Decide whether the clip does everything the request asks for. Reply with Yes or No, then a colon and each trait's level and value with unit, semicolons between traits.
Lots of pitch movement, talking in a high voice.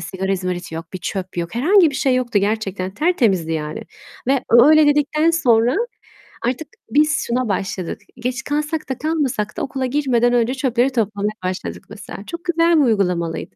Yes: wide, 7.2 semitones; high, 240 Hz